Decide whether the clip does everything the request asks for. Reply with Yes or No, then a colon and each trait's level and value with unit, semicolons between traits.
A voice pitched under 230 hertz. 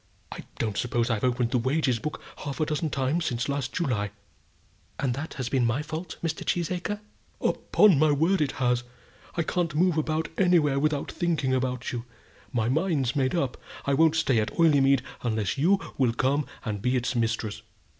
Yes: medium, 140 Hz